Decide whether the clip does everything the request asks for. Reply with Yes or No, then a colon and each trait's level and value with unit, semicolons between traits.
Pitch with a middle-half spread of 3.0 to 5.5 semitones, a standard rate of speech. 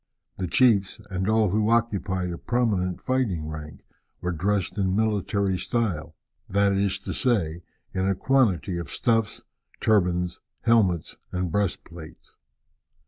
No: average, 3.5 semitones; slow, 130 wpm